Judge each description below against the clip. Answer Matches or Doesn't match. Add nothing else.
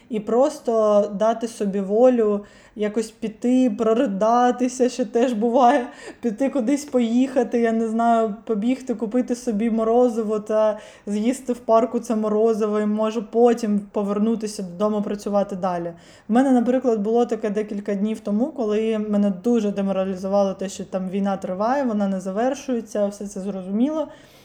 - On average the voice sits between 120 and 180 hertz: Doesn't match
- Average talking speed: Matches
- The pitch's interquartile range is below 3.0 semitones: Matches